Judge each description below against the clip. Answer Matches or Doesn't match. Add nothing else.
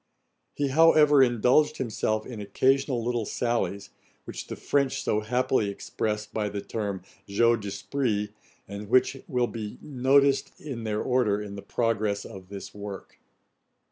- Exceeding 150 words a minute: Doesn't match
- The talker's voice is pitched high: Doesn't match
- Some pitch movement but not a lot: Matches